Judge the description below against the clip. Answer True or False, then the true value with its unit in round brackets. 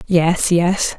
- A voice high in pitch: False (175 Hz)